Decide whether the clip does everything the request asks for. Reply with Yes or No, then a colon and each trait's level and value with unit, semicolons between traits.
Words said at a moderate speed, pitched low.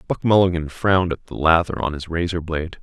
Yes: average, 190 wpm; very low, 85 Hz